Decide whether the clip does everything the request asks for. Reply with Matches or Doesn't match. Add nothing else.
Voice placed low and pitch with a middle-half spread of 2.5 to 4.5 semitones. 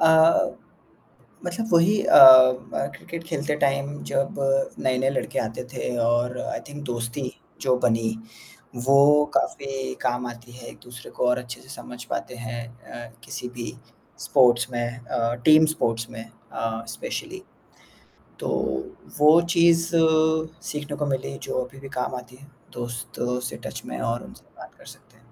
Matches